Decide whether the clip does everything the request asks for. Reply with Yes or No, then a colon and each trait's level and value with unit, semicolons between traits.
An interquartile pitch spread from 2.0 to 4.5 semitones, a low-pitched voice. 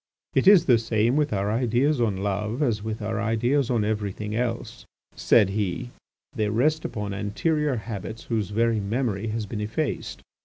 Yes: average, 2.9 semitones; low, 110 Hz